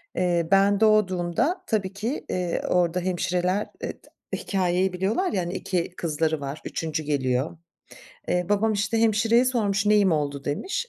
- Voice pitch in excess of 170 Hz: Yes, medium, 185 Hz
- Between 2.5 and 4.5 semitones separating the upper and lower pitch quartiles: Yes, average, 3.8 semitones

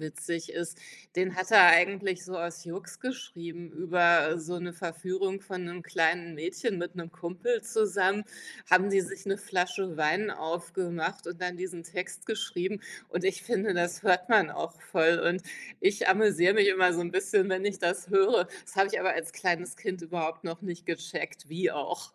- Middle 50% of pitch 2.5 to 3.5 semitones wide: No, narrow, 2.1 semitones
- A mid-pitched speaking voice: Yes, medium, 180 Hz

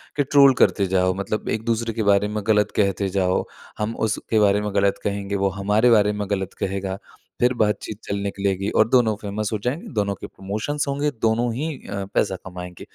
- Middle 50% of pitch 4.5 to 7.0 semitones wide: No, narrow, 2.4 semitones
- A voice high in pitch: No, low, 105 Hz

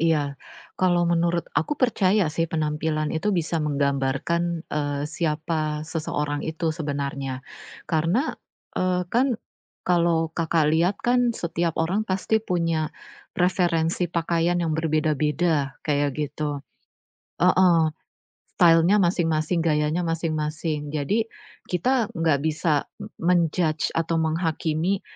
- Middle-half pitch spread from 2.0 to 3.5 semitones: Yes, narrow, 2.4 semitones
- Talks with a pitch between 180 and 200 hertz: No, medium, 165 Hz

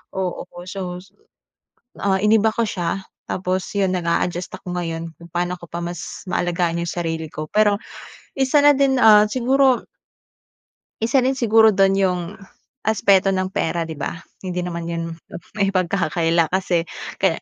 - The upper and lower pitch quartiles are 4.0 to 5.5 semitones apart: No, average, 3.4 semitones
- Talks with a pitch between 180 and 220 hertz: Yes, medium, 185 Hz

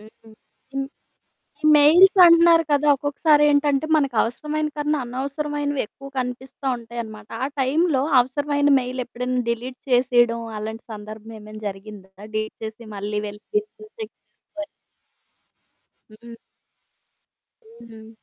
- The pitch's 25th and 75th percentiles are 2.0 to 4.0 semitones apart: No, average, 4.8 semitones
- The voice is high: Yes, very high, 255 Hz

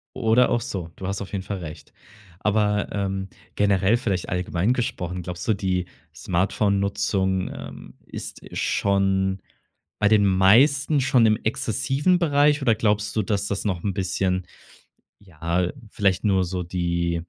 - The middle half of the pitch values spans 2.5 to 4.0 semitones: Yes, average, 2.8 semitones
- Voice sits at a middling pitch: No, low, 100 Hz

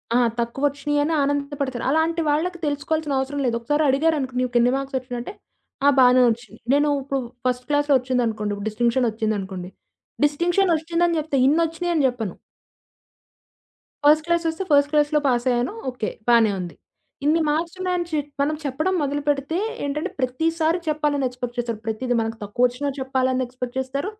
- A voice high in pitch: Yes, very high, 275 Hz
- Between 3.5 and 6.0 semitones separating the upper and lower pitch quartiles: Yes, average, 4.0 semitones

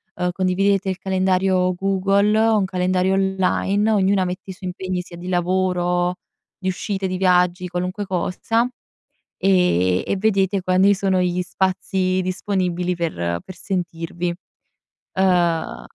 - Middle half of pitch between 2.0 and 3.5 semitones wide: No, narrow, 1.3 semitones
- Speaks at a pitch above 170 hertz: Yes, medium, 185 Hz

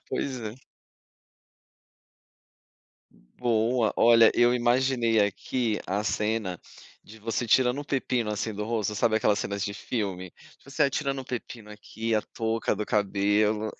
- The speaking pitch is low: Yes, low, 110 Hz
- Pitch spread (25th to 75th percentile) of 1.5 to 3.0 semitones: Yes, narrow, 2.5 semitones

